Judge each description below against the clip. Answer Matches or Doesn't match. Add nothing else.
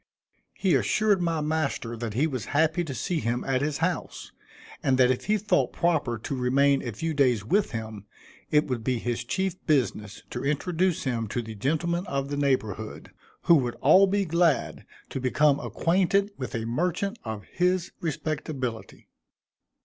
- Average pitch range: Doesn't match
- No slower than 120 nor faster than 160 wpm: Doesn't match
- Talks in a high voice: Doesn't match